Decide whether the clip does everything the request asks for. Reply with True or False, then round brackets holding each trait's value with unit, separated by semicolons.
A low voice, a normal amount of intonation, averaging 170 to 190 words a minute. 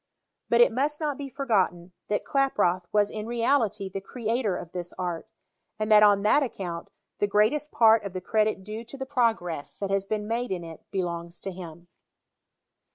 False (210 Hz; 4.4 semitones; 185 wpm)